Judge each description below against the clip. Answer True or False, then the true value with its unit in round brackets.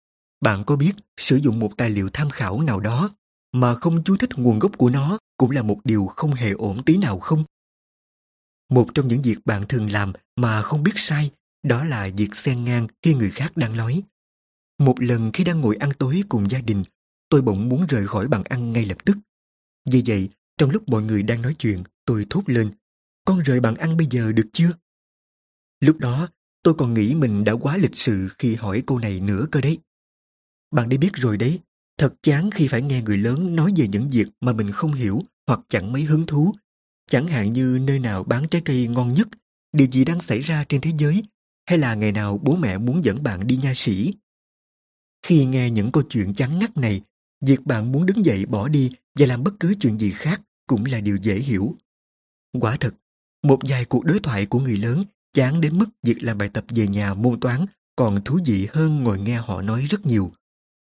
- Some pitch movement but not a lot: False (6.1 semitones)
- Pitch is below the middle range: True (130 Hz)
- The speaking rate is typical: True (220 wpm)